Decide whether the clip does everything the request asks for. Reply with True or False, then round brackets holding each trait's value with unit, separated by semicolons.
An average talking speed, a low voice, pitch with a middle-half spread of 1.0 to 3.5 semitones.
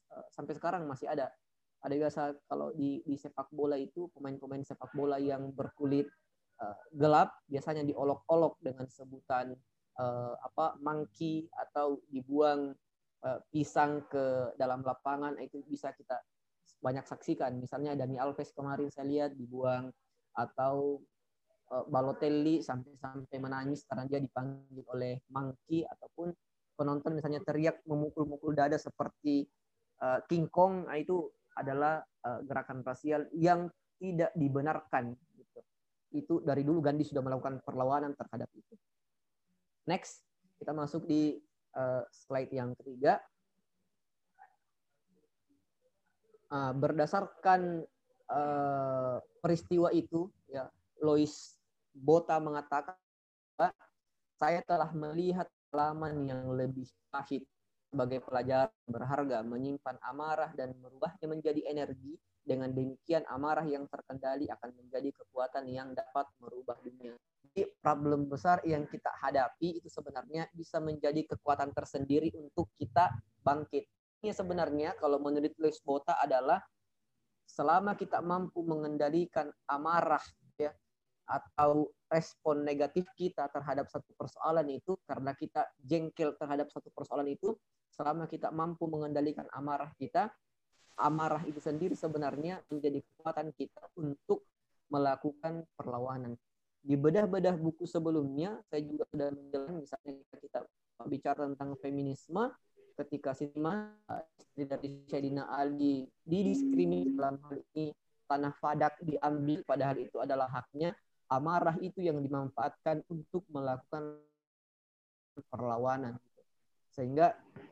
False (110 wpm; 145 Hz; 2.8 semitones)